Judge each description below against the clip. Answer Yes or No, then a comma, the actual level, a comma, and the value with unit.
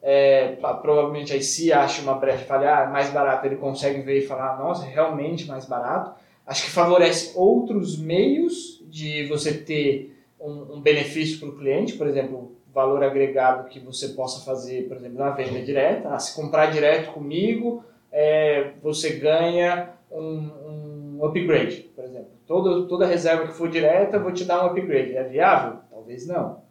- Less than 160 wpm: No, average, 180 wpm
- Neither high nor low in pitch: Yes, medium, 150 Hz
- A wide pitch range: No, average, 3.5 semitones